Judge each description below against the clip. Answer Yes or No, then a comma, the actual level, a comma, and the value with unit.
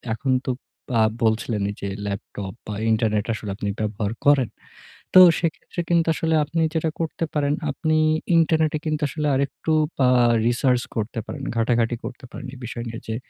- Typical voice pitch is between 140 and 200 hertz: No, low, 125 Hz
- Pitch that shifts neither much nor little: No, wide, 5.8 semitones